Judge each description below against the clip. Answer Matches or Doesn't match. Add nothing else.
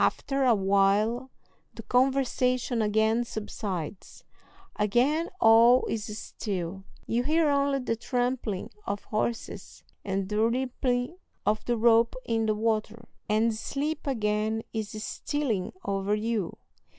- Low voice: Doesn't match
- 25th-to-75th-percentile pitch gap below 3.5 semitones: Matches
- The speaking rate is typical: Doesn't match